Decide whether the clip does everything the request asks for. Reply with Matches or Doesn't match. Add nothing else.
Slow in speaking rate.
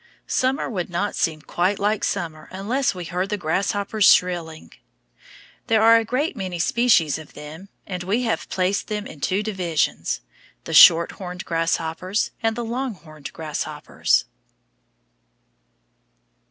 Matches